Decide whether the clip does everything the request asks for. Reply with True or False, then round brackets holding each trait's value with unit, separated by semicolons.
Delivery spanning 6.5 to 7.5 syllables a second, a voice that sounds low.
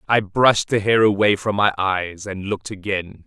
False (4.9 syllables/s; 100 Hz)